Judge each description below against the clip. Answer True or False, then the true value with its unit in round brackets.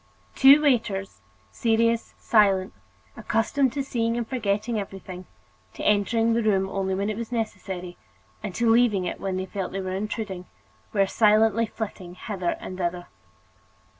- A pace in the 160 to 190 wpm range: False (150 wpm)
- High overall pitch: True (210 Hz)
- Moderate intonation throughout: True (3.2 semitones)